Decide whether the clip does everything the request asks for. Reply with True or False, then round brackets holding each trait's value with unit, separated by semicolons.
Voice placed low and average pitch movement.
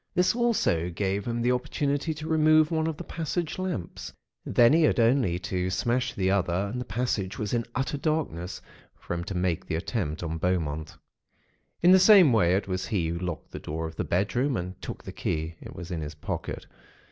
False (100 Hz; 8.5 semitones)